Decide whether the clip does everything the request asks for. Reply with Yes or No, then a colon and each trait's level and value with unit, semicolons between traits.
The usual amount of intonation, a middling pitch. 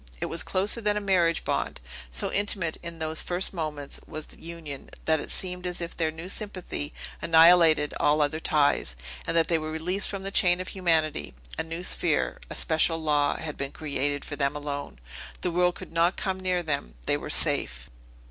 Yes: average, 3.0 semitones; medium, 165 Hz